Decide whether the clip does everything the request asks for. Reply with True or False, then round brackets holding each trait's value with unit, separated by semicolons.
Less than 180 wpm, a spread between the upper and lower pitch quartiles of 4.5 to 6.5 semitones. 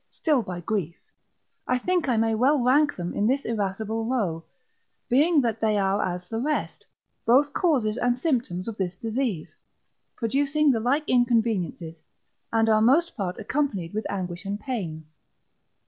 True (155 wpm; 5.2 semitones)